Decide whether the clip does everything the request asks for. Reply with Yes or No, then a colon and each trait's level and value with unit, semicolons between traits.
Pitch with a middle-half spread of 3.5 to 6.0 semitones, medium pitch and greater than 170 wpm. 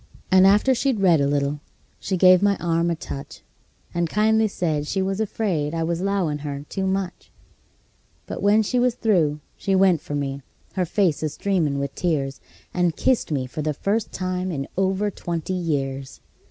Yes: average, 4.8 semitones; medium, 175 Hz; average, 180 wpm